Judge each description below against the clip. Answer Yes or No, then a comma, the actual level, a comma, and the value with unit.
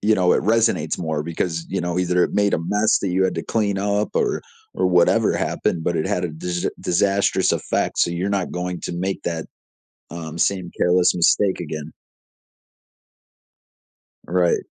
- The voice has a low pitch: Yes, very low, 90 Hz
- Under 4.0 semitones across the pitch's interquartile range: Yes, narrow, 2.4 semitones